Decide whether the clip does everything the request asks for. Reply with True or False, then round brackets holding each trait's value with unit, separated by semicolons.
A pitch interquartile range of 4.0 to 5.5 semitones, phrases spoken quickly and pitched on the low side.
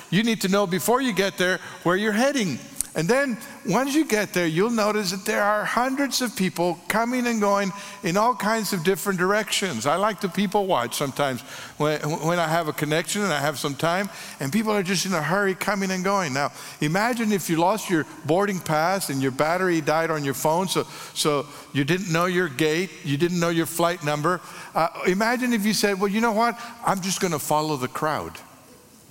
False (4.5 semitones; 215 wpm; 190 Hz)